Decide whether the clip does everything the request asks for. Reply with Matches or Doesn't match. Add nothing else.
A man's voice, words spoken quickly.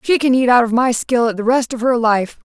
Doesn't match